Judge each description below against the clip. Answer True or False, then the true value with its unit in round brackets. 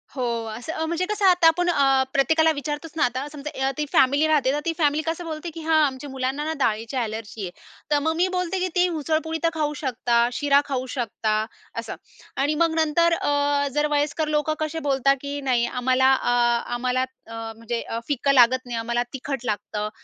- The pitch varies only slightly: False (4.0 semitones)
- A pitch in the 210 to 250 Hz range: False (285 Hz)